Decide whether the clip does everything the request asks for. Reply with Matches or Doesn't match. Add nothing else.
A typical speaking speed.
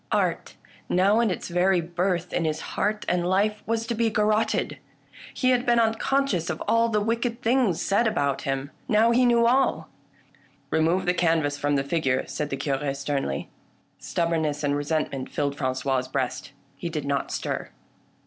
Matches